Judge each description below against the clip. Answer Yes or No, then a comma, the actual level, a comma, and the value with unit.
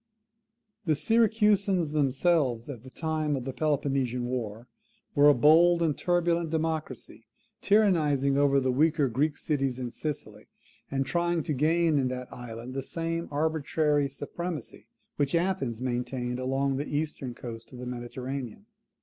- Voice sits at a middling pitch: Yes, medium, 145 Hz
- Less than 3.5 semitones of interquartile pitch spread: No, average, 4.1 semitones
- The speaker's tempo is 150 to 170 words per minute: No, average, 140 wpm